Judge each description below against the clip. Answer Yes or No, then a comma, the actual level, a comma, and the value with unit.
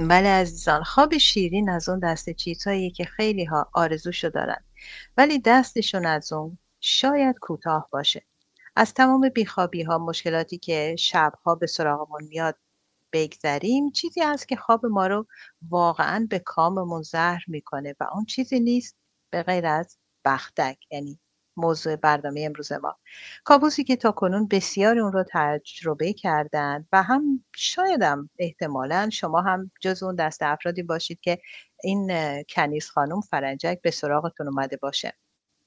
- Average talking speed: Yes, average, 145 wpm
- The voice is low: No, medium, 175 Hz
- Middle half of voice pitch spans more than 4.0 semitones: Yes, average, 4.8 semitones